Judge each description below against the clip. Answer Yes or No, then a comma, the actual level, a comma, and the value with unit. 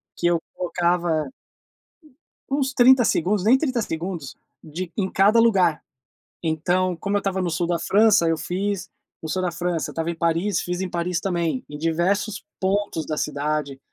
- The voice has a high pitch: No, medium, 175 Hz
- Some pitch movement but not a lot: Yes, average, 3.3 semitones